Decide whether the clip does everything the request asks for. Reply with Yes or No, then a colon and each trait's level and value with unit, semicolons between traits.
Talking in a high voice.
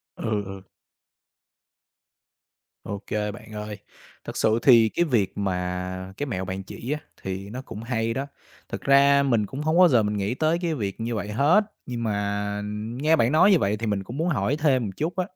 No: low, 115 Hz